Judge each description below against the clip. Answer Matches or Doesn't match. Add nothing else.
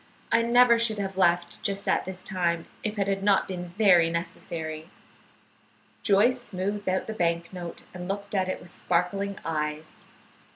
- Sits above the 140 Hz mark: Matches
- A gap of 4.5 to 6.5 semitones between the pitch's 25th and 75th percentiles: Doesn't match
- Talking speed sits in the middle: Matches